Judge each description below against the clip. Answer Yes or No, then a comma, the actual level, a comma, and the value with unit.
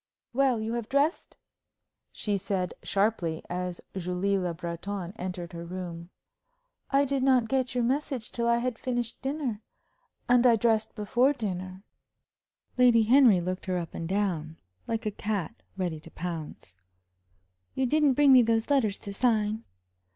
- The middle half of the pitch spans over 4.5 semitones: Yes, wide, 5.4 semitones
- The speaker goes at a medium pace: Yes, average, 150 wpm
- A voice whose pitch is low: No, high, 215 Hz